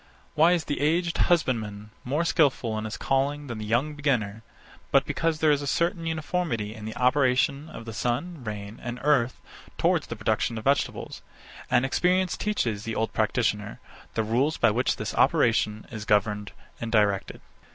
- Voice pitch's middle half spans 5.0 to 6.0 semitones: Yes, wide, 5.5 semitones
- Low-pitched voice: Yes, low, 125 Hz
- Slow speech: No, average, 170 wpm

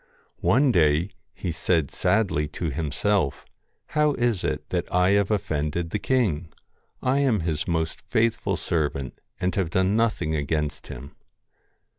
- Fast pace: No, average, 145 wpm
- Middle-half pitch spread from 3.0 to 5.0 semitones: No, wide, 5.4 semitones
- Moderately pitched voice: No, very low, 85 Hz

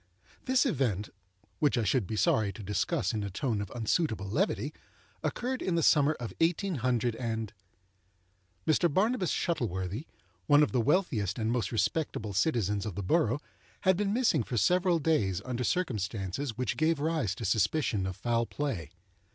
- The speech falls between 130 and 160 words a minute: Yes, average, 145 wpm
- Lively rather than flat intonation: Yes, wide, 7.9 semitones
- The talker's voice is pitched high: No, low, 120 Hz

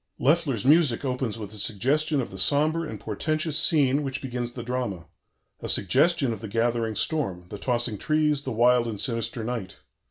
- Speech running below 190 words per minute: Yes, average, 180 wpm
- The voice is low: Yes, low, 125 Hz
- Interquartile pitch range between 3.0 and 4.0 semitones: No, average, 4.6 semitones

